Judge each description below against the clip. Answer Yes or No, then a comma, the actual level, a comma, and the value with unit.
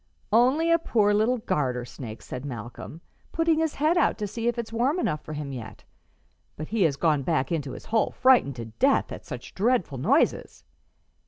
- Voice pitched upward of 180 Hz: Yes, high, 190 Hz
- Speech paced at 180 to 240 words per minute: Yes, average, 190 wpm